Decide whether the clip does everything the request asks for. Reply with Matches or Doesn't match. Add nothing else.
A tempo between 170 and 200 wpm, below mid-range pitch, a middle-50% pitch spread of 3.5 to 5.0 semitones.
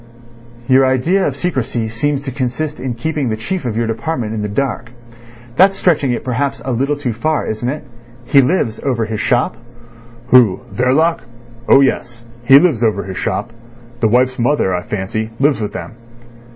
Matches